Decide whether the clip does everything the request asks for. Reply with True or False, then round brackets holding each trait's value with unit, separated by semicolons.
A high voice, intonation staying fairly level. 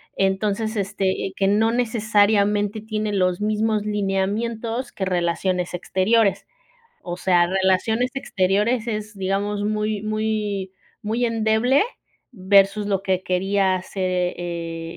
True (205 Hz; 2.3 semitones)